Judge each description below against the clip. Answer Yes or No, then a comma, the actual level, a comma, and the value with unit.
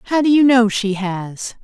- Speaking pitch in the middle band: No, high, 230 Hz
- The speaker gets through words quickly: Yes, fast, 220 wpm